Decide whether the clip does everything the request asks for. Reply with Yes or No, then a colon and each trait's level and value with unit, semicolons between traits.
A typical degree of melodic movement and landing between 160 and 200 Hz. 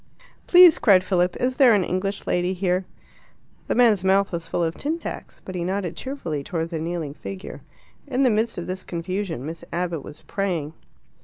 Yes: average, 3.2 semitones; medium, 185 Hz